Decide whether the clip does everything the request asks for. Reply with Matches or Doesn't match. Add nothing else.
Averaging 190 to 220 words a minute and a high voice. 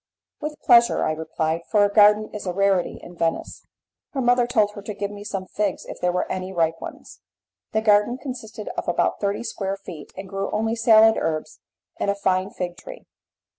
Matches